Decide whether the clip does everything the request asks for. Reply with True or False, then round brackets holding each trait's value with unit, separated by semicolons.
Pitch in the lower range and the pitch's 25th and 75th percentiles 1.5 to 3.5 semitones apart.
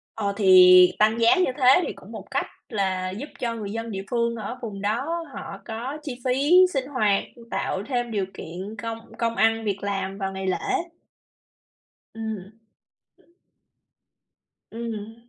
False (220 Hz; 3.2 semitones)